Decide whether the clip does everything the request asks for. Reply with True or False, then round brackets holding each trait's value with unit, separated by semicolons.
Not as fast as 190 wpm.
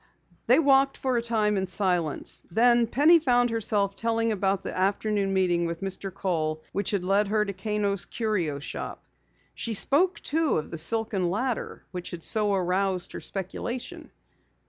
True (165 wpm)